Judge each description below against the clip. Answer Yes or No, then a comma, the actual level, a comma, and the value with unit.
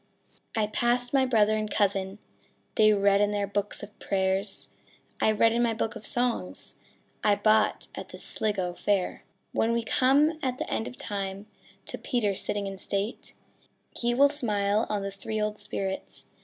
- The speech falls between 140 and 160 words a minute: No, average, 170 wpm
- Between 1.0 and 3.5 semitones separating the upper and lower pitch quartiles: Yes, average, 2.7 semitones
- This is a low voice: No, high, 210 Hz